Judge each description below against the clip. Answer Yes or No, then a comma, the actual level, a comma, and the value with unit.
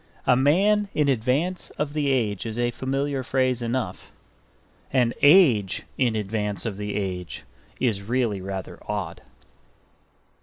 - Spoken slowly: Yes, slow, 130 wpm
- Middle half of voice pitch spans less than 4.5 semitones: No, average, 4.9 semitones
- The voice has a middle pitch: No, low, 125 Hz